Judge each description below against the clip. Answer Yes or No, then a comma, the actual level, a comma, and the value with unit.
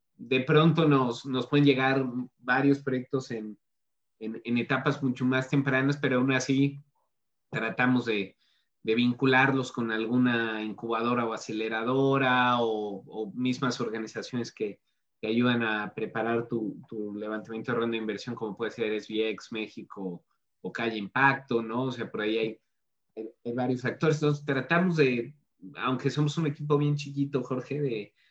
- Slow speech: No, average, 155 wpm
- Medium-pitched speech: No, low, 125 Hz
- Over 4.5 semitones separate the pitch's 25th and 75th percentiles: No, average, 3.4 semitones